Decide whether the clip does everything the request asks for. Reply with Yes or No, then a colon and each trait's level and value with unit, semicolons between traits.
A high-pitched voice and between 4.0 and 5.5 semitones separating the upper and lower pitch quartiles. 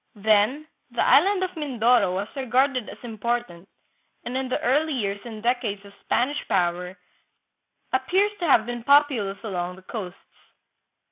Yes: high, 240 Hz; average, 5.1 semitones